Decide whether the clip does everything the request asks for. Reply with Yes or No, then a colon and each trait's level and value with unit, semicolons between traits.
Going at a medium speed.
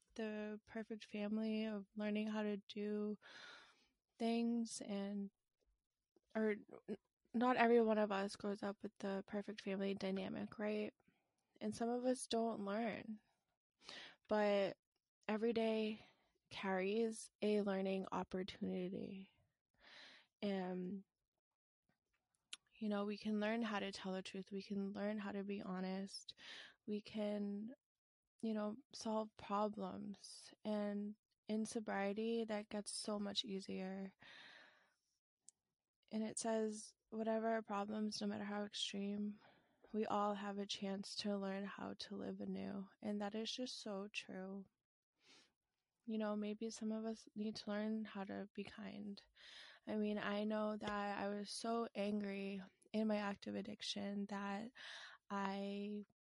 No: slow, 130 wpm